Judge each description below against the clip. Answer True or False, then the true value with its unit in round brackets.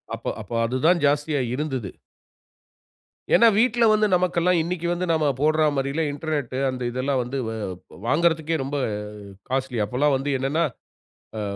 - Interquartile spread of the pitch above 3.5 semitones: True (4.2 semitones)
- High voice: False (145 Hz)